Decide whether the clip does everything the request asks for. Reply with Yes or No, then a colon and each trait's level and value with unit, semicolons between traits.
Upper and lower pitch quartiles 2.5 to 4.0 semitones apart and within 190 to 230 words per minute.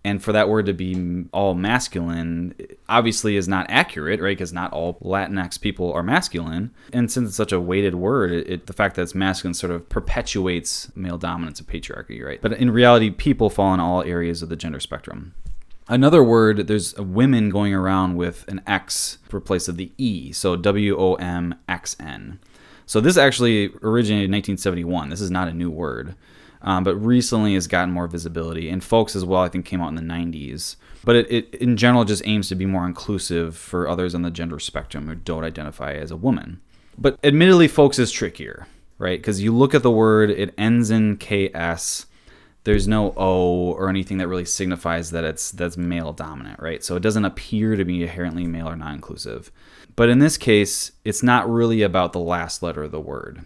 Yes: average, 3.6 semitones; average, 200 wpm